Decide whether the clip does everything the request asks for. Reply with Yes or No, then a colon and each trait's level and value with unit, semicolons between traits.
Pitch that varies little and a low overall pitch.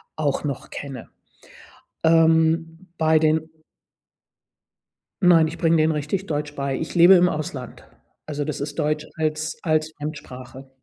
No: narrow, 1.8 semitones; medium, 155 Hz